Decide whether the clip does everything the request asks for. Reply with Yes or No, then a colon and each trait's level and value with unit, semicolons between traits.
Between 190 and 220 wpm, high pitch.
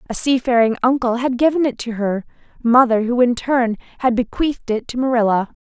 No: average, 180 wpm; high, 240 Hz